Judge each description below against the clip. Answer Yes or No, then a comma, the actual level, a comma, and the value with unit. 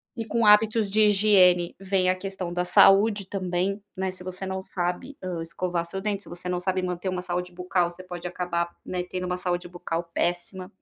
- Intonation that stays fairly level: Yes, narrow, 1.6 semitones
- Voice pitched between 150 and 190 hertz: Yes, medium, 185 Hz